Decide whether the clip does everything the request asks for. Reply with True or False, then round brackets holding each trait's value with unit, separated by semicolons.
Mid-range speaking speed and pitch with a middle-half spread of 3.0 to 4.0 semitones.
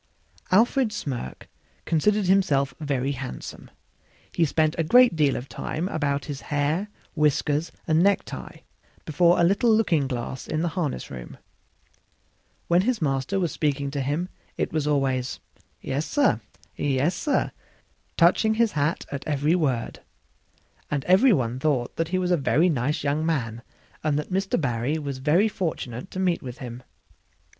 False (150 wpm; 4.7 semitones)